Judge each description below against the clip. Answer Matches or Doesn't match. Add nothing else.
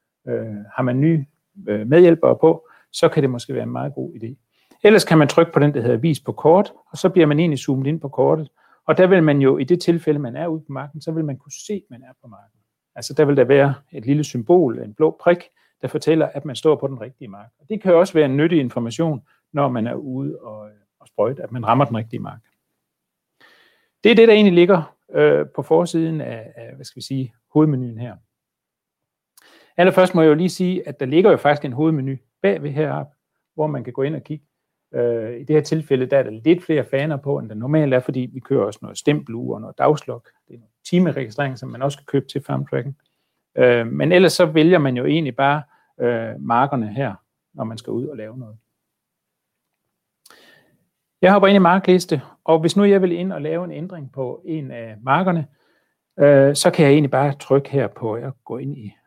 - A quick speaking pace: Matches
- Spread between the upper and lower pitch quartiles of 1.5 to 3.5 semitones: Doesn't match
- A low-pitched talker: Doesn't match